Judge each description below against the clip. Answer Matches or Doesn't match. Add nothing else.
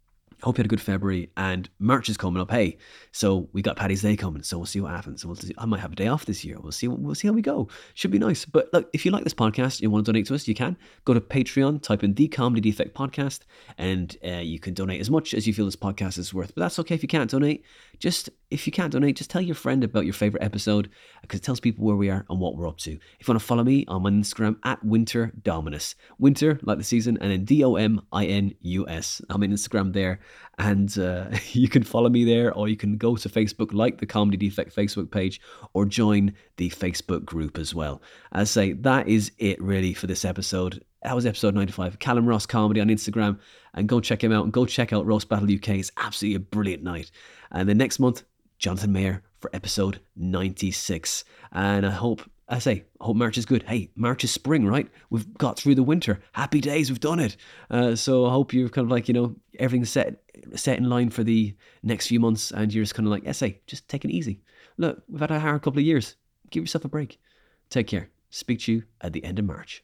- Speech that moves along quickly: Matches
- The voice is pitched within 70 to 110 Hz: Matches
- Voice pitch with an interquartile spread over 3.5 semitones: Matches